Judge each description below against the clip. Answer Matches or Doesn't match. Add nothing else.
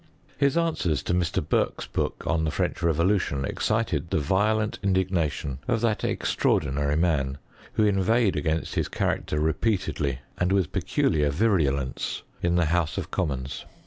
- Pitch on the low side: Matches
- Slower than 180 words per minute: Matches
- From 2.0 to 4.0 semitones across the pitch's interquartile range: Doesn't match